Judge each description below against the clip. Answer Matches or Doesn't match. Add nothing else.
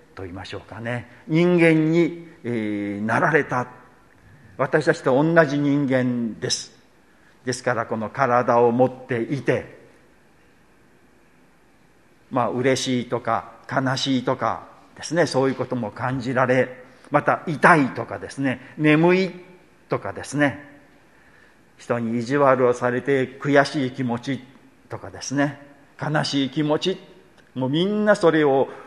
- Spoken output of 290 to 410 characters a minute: Doesn't match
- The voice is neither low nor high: Doesn't match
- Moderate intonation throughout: Matches